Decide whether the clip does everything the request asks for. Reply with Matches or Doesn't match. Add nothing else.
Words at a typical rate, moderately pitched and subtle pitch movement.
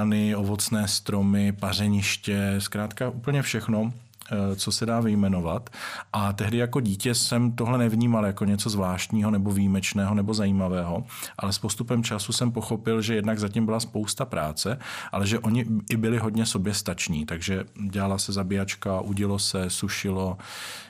Doesn't match